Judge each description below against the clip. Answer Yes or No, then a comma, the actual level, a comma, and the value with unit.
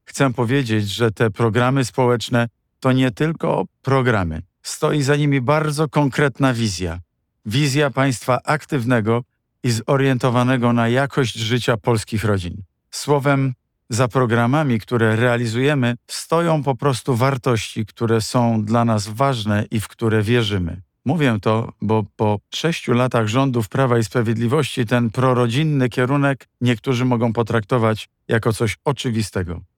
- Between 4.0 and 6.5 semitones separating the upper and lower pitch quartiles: No, average, 3.3 semitones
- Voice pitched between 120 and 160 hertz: Yes, low, 125 Hz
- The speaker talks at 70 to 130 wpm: Yes, average, 125 wpm